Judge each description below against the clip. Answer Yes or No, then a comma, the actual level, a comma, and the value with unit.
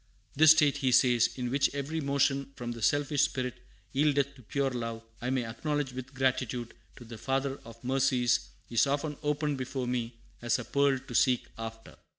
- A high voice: No, low, 130 Hz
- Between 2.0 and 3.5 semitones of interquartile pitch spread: Yes, narrow, 2.5 semitones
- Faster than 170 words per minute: Yes, average, 180 wpm